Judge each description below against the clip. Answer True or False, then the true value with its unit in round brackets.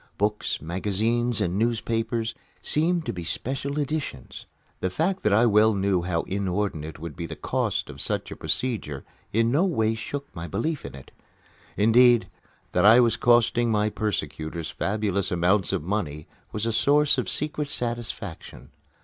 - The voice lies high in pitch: False (110 Hz)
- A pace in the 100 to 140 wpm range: False (160 wpm)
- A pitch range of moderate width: True (4.7 semitones)